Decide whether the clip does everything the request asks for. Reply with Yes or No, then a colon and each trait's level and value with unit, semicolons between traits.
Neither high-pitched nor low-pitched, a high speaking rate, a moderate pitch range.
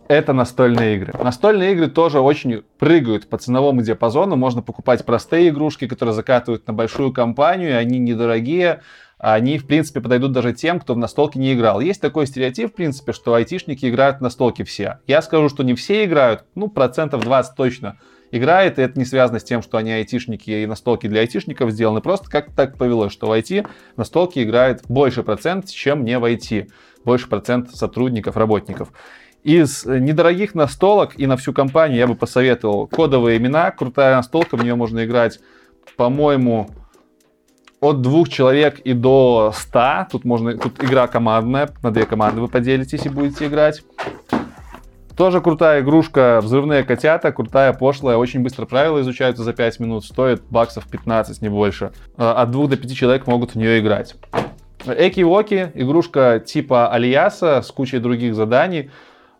No: low, 125 Hz; fast, 165 wpm; average, 3.9 semitones